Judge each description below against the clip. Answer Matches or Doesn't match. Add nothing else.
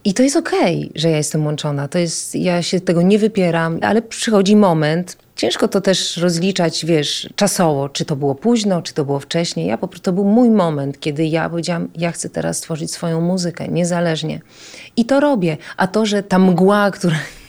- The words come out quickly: Matches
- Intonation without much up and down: Doesn't match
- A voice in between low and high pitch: Matches